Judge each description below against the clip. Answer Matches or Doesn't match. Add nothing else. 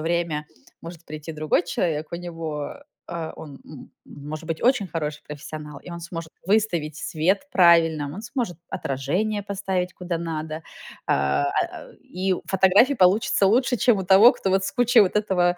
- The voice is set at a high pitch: Doesn't match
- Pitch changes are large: Doesn't match